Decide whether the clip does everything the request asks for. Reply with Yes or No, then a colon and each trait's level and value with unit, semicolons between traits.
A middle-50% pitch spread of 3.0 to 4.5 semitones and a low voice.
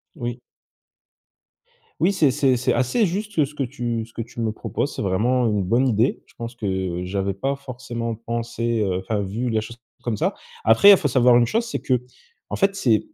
Yes: average, 3.4 semitones; low, 120 Hz